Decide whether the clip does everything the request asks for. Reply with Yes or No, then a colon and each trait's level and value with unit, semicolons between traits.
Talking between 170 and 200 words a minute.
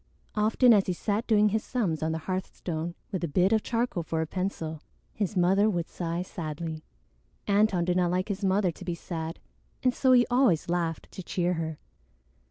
Yes: average, 190 wpm